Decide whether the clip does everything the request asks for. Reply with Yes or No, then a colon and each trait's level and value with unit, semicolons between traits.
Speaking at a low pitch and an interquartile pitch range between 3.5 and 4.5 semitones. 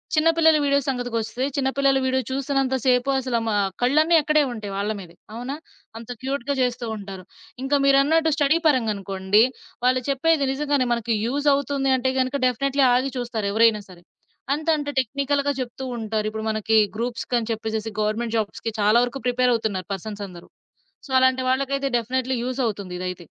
No: very high, 250 Hz; average, 4.0 semitones